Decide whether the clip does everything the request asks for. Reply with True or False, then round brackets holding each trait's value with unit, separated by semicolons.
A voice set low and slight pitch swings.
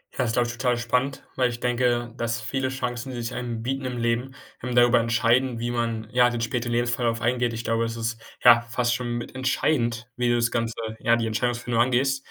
True (120 Hz; 1.1 semitones)